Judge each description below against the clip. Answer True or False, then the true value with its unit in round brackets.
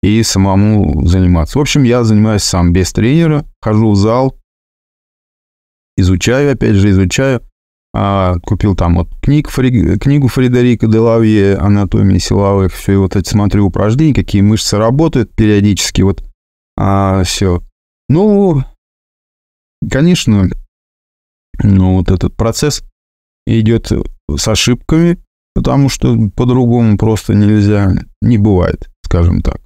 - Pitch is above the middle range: False (105 Hz)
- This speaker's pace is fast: False (120 wpm)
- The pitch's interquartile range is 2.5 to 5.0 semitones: True (4.5 semitones)